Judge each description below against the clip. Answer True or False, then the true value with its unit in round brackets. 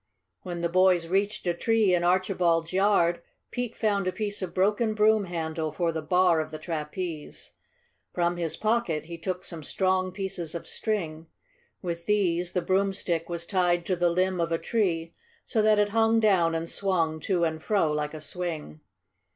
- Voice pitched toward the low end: False (180 Hz)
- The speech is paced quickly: False (180 wpm)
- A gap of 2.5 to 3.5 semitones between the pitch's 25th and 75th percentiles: True (2.9 semitones)